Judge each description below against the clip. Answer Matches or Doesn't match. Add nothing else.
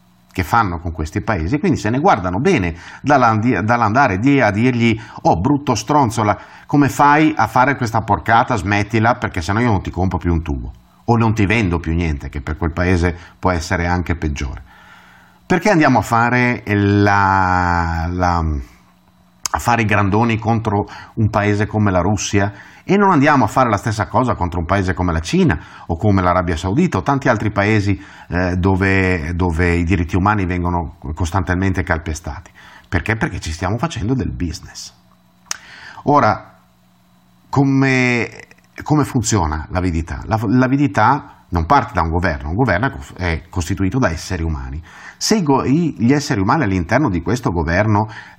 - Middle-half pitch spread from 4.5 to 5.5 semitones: Matches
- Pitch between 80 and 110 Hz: Matches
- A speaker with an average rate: Matches